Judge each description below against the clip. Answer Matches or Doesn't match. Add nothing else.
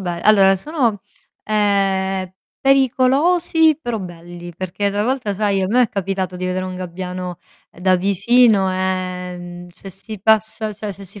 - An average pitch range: Matches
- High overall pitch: Matches